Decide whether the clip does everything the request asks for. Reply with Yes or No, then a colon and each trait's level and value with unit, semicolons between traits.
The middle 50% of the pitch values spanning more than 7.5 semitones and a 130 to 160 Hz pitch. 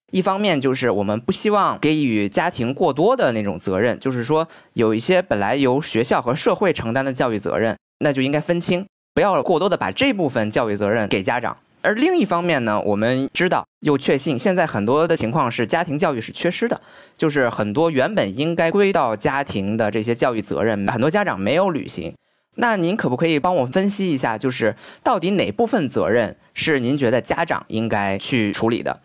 Yes: wide, 8.0 semitones; medium, 140 Hz